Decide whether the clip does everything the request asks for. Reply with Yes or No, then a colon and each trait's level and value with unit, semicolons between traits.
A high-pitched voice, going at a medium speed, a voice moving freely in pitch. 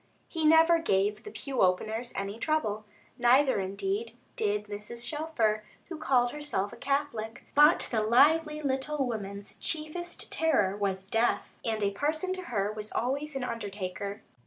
Yes: high, 235 Hz; average, 150 wpm; wide, 6.6 semitones